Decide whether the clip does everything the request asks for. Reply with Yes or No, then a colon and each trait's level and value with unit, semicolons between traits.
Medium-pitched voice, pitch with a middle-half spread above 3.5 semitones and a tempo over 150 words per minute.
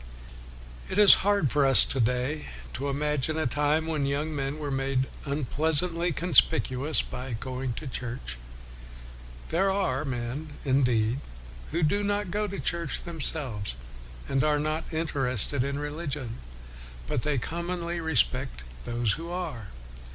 No: medium, 145 Hz; average, 4.1 semitones; average, 140 wpm